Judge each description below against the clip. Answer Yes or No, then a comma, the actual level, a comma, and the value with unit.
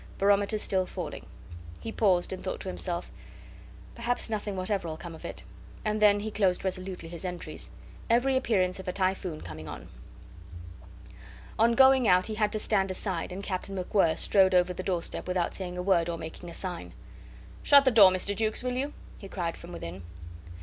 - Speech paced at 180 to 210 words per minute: Yes, average, 185 wpm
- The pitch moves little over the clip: No, average, 3.0 semitones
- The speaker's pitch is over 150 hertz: Yes, high, 190 Hz